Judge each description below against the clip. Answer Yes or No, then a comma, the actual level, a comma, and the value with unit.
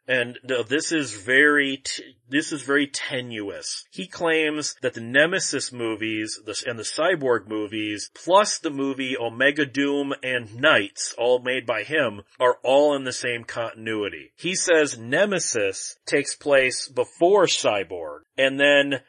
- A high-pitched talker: No, low, 135 Hz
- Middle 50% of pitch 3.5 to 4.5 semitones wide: Yes, average, 3.9 semitones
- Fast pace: No, average, 150 wpm